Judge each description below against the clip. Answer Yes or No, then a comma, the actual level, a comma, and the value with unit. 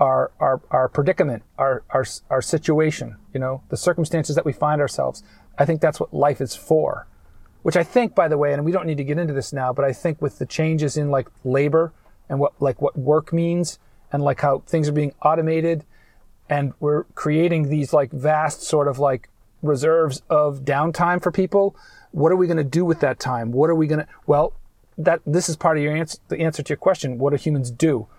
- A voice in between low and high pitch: Yes, medium, 150 Hz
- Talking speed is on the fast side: Yes, fast, 225 wpm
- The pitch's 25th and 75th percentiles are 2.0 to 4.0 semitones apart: Yes, average, 2.8 semitones